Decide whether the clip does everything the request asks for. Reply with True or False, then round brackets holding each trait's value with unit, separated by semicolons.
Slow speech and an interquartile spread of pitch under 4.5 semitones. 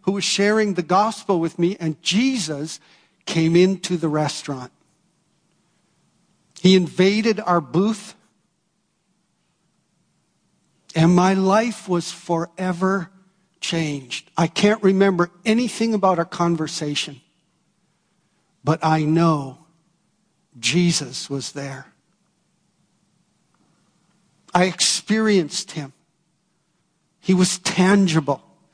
True (90 wpm; 2.7 semitones)